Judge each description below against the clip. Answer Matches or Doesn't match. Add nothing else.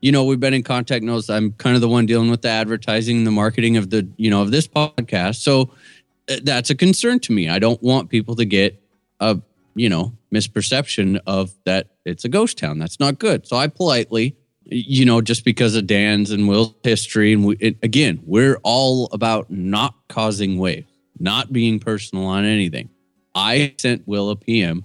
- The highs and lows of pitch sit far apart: Doesn't match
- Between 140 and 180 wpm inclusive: Doesn't match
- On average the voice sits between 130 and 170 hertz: Doesn't match